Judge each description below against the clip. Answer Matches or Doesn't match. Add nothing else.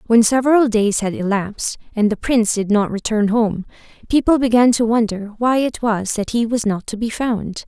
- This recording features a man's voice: Doesn't match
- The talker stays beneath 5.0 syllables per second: Doesn't match